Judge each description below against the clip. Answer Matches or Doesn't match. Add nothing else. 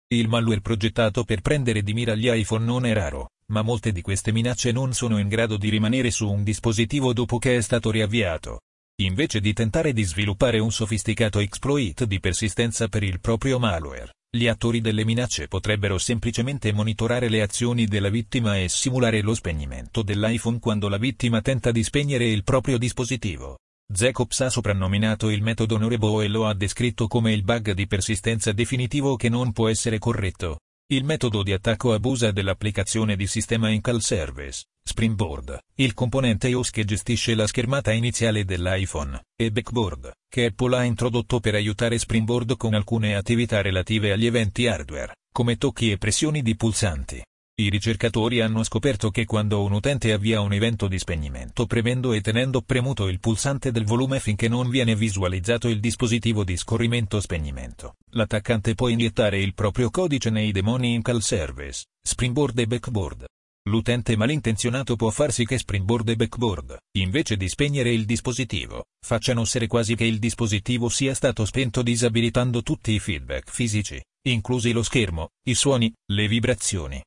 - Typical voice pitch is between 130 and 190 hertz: Doesn't match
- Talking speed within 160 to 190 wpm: Matches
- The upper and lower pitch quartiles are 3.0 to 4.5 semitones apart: Doesn't match